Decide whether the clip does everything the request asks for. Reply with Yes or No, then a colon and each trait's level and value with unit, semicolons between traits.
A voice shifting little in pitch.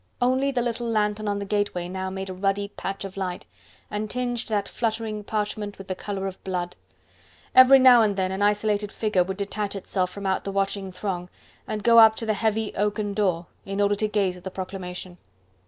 Yes: narrow, 2.1 semitones